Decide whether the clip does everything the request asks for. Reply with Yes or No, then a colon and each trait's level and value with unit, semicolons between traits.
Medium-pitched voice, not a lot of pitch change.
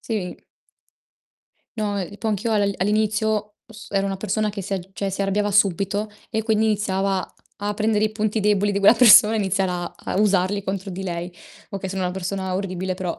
No: high, 200 Hz; narrow, 1.8 semitones